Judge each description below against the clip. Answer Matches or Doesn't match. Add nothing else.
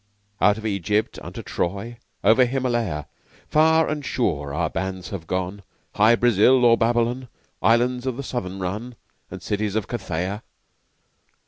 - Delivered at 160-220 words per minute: Doesn't match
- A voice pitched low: Matches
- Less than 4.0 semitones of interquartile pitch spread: Doesn't match